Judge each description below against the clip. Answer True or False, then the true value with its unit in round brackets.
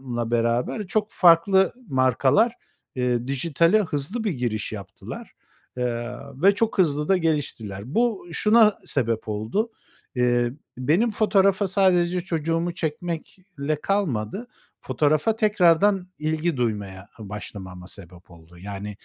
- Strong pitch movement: True (8.3 semitones)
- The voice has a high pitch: False (150 Hz)